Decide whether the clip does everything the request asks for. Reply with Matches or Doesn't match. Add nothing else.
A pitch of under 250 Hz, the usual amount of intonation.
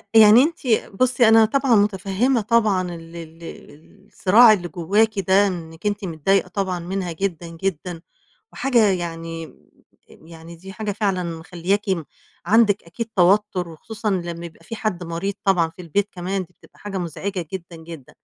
Matches